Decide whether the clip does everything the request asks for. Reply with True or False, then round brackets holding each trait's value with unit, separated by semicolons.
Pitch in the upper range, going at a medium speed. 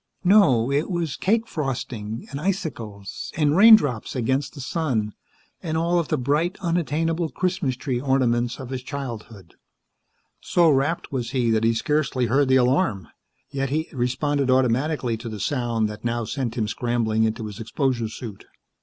False (130 Hz; 160 wpm)